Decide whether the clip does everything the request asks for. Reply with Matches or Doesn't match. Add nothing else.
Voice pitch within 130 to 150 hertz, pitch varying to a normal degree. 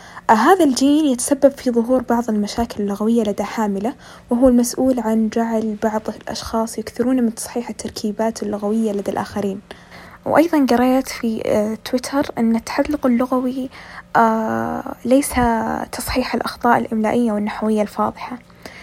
Doesn't match